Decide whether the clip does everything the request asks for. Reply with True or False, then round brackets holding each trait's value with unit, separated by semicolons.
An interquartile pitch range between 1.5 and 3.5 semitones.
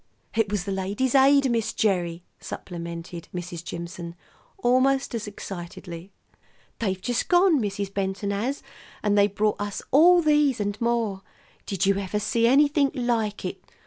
False (4.7 semitones)